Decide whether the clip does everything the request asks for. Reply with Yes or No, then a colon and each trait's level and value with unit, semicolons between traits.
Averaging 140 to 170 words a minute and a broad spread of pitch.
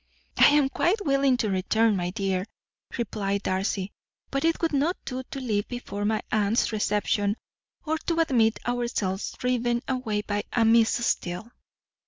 No: average, 155 wpm; average, 4.2 semitones